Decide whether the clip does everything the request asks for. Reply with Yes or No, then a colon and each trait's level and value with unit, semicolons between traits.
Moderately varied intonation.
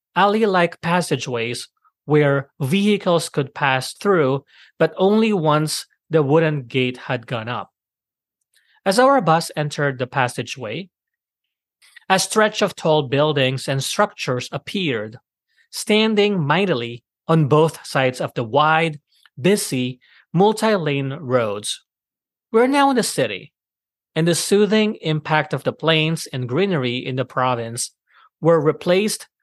No: wide, 6.3 semitones